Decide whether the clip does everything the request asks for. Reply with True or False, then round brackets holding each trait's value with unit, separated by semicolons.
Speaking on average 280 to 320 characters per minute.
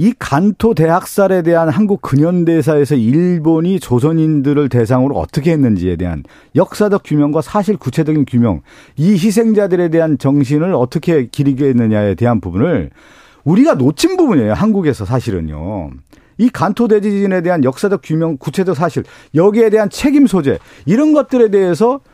False (360 characters per minute)